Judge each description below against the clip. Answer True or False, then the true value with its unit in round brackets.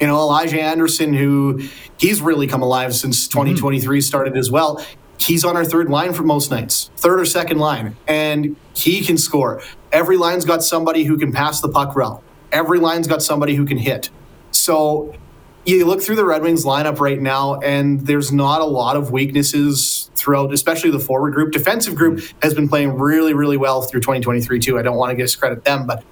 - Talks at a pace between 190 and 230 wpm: True (200 wpm)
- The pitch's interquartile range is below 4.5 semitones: True (2.8 semitones)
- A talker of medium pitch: True (145 Hz)